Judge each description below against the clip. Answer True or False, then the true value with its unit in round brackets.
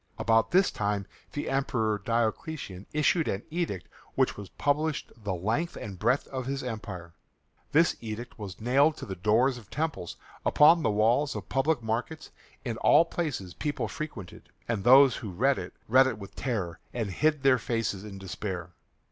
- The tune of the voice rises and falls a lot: True (5.7 semitones)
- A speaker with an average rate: True (170 wpm)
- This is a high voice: False (115 Hz)